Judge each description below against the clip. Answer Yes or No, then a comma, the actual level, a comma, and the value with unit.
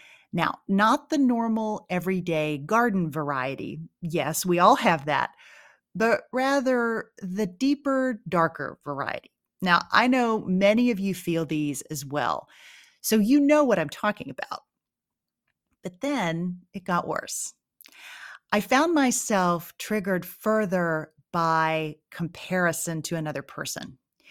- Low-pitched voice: No, medium, 185 Hz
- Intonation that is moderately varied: No, wide, 6.0 semitones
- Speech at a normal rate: No, slow, 125 wpm